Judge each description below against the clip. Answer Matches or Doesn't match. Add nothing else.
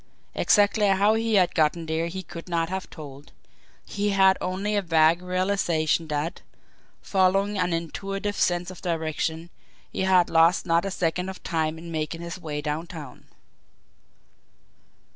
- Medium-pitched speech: Matches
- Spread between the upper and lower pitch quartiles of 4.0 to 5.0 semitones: Doesn't match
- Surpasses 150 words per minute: Doesn't match